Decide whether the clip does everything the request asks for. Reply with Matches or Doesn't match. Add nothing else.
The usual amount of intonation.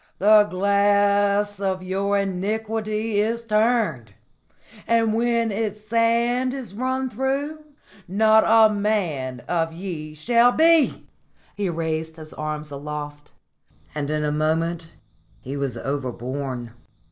Doesn't match